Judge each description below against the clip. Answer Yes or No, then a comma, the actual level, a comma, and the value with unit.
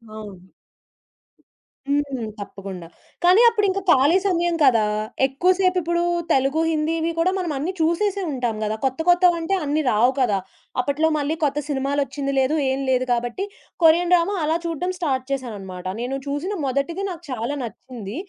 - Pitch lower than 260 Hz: No, very high, 285 Hz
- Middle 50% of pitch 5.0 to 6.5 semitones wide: Yes, average, 5.3 semitones